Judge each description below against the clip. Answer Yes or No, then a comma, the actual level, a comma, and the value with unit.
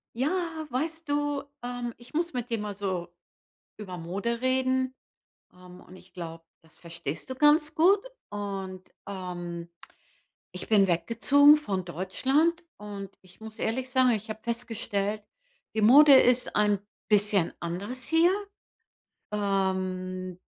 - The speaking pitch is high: Yes, high, 215 Hz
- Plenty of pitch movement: Yes, wide, 5.8 semitones